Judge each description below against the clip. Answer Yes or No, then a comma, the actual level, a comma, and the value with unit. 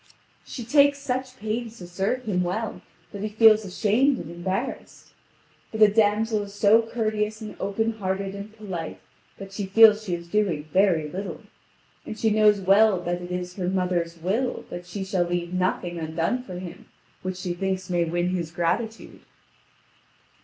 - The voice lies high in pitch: Yes, high, 195 Hz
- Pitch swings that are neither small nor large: Yes, average, 3.5 semitones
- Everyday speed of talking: Yes, average, 170 wpm